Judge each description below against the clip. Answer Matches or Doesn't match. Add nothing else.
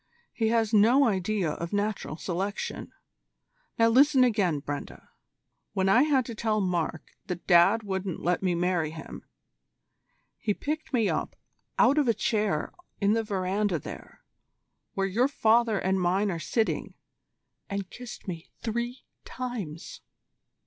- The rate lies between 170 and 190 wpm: Doesn't match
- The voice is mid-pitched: Doesn't match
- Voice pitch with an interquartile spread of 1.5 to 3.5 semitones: Doesn't match